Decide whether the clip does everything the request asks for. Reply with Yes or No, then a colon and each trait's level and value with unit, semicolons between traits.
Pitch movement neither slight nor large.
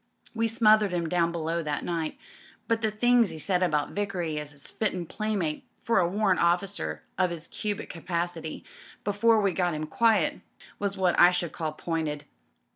Yes: average, 4.2 semitones